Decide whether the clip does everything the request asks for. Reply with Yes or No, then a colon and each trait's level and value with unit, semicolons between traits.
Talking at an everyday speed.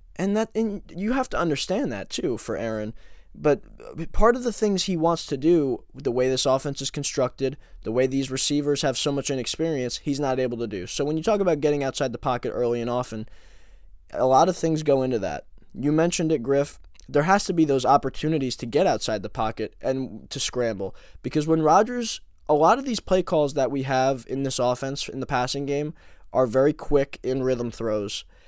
No: fast, 215 wpm